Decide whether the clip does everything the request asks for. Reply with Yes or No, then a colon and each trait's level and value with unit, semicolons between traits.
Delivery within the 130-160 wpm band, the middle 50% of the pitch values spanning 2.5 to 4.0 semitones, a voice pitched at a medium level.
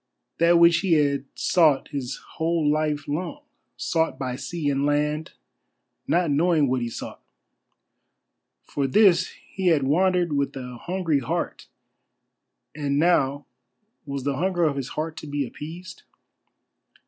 Yes: slow, 135 wpm; average, 3.4 semitones; medium, 150 Hz